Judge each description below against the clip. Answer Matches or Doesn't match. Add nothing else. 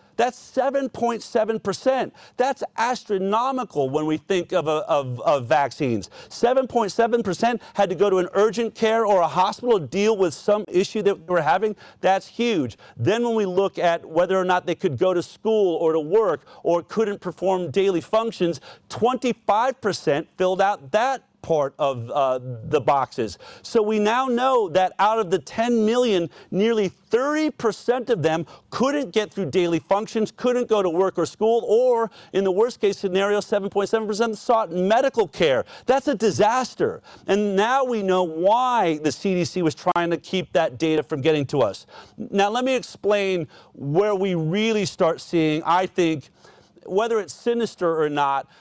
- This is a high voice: Matches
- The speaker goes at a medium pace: Matches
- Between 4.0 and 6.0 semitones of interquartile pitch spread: Matches